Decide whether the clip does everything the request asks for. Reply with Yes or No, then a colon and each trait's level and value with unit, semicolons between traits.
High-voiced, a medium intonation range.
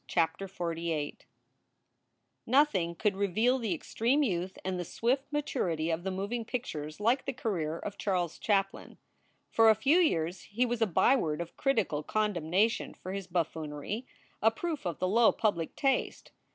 No: high, 195 Hz; wide, 5.7 semitones